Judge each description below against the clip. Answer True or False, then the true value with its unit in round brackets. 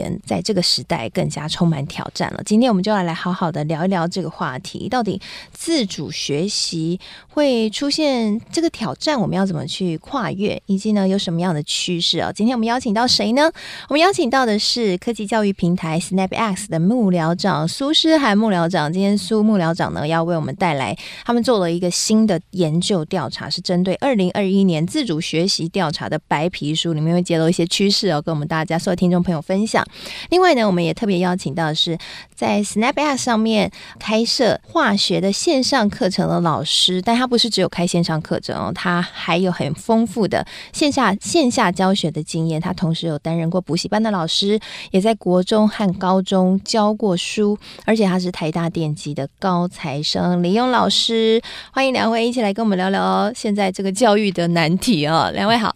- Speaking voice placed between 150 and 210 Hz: True (190 Hz)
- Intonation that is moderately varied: True (4.4 semitones)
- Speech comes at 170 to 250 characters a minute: False (315 characters per minute)